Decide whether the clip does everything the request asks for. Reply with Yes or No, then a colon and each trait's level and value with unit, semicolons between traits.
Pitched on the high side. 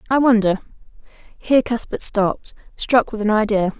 Yes: high, 220 Hz